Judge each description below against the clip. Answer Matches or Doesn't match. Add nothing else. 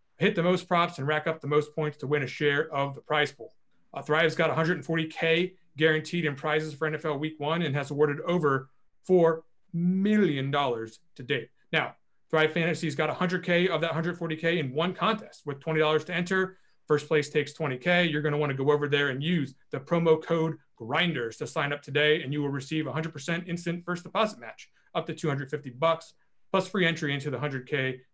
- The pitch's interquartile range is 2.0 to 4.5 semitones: Matches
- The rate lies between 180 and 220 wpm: Matches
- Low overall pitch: Doesn't match